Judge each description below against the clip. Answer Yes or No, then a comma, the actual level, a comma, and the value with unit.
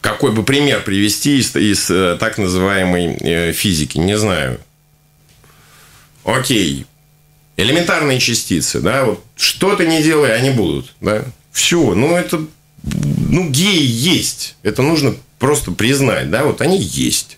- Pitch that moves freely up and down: Yes, wide, 6.4 semitones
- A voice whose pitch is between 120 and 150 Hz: Yes, low, 135 Hz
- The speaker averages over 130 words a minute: No, average, 120 wpm